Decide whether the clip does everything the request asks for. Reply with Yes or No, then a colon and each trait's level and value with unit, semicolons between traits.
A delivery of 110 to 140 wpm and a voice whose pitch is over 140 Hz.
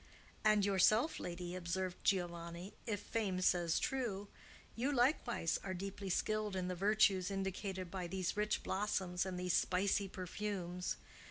Yes: slow, 135 wpm; high, 190 Hz